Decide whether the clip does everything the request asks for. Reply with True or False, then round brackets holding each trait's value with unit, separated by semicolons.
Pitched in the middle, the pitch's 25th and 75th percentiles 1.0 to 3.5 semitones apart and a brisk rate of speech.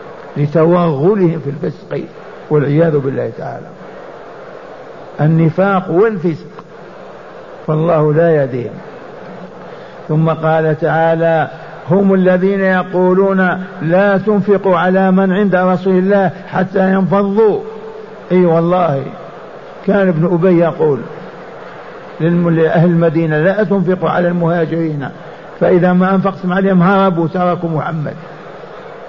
False (175 Hz; 2.8 semitones; 95 wpm)